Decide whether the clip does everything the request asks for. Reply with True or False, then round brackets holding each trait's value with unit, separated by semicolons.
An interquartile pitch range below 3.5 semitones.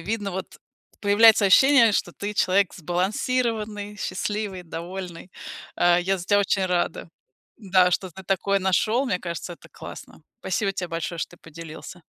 True (2.8 semitones)